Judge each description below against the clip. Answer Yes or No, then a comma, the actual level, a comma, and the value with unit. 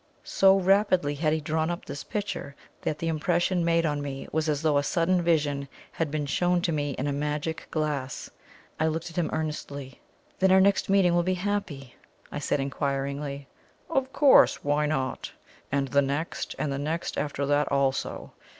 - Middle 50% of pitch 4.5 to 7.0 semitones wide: No, average, 3.5 semitones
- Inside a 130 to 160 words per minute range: No, average, 185 wpm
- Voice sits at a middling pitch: Yes, medium, 155 Hz